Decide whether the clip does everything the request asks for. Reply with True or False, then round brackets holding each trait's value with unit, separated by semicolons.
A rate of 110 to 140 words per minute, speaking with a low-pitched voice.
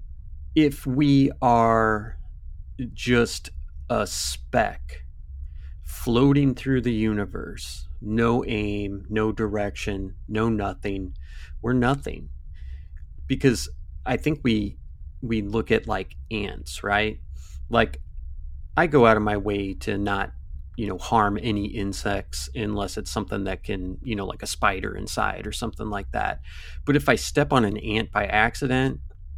True (135 wpm; 100 Hz)